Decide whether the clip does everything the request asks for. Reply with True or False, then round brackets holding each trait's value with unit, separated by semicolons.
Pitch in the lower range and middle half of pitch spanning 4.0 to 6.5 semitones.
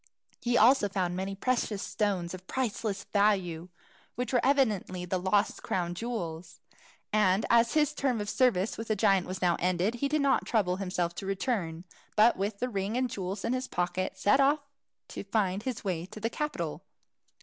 False (205 Hz; 4.5 semitones)